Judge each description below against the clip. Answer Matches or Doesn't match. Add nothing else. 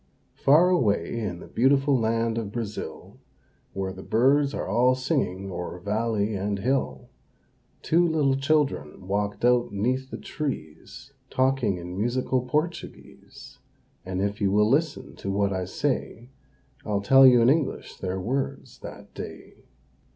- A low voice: Matches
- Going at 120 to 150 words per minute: Matches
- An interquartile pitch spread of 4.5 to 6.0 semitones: Matches